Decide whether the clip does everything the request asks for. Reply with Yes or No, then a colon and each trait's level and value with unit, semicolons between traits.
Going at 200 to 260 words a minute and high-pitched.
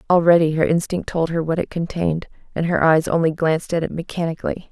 No: fast, 205 wpm; medium, 165 Hz